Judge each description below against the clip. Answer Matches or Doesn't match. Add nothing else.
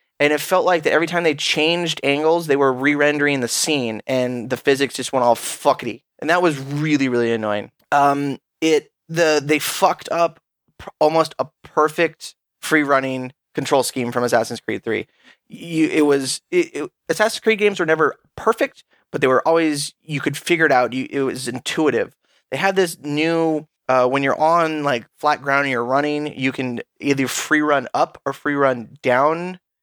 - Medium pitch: Matches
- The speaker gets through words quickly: Doesn't match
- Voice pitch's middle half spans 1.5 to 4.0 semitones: Matches